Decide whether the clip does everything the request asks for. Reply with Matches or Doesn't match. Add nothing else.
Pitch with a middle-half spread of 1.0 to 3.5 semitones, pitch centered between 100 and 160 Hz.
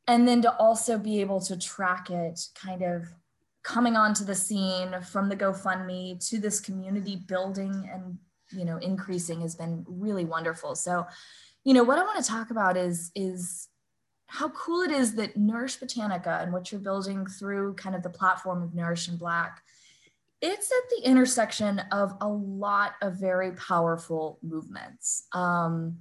Doesn't match